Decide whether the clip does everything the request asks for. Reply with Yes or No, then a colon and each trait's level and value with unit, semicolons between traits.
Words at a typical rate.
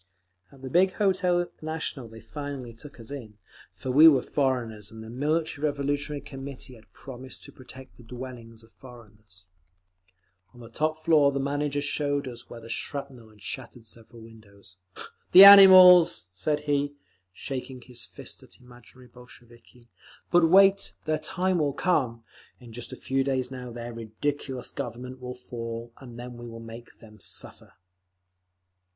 Yes: average, 155 wpm